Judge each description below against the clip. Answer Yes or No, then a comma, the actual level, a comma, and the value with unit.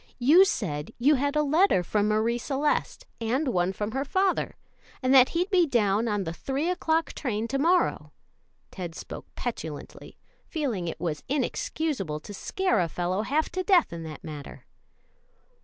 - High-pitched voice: Yes, high, 245 Hz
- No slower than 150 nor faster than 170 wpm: Yes, average, 165 wpm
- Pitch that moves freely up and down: Yes, wide, 8.5 semitones